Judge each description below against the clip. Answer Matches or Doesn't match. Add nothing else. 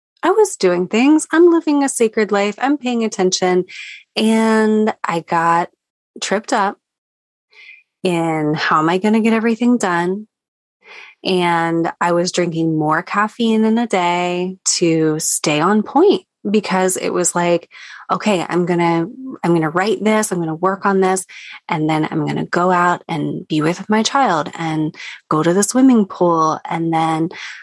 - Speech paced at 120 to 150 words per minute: Doesn't match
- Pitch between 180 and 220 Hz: Matches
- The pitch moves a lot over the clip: Doesn't match